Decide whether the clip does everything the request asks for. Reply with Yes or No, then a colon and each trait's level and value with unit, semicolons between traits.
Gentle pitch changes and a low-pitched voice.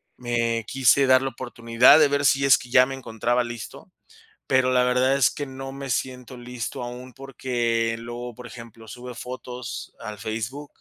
Yes: narrow, 1.9 semitones; low, 125 Hz